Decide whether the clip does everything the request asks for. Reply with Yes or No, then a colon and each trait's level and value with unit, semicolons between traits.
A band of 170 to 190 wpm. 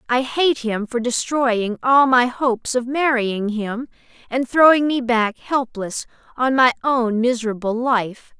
No: average, 150 wpm